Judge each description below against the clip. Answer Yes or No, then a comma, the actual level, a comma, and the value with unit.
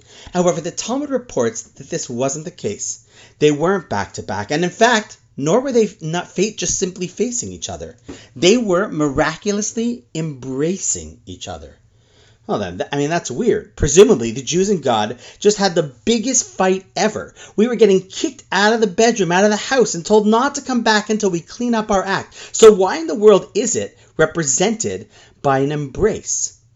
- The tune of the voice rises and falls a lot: Yes, wide, 8.8 semitones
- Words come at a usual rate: Yes, average, 190 wpm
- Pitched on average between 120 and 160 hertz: No, medium, 175 Hz